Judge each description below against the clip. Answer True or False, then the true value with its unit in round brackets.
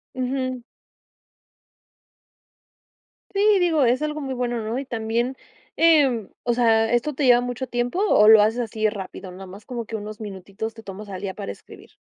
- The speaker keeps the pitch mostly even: False (3.3 semitones)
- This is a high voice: True (235 Hz)